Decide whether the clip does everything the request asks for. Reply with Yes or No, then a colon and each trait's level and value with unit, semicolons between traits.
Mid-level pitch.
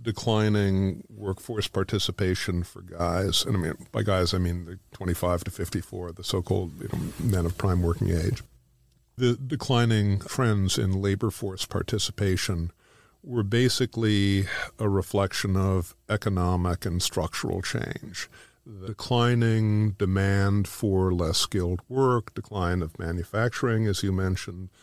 No: low, 100 Hz